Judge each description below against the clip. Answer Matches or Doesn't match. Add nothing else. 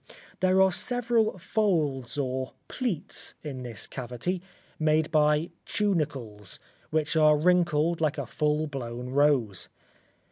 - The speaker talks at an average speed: Doesn't match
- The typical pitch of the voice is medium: Matches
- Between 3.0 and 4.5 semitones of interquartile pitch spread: Doesn't match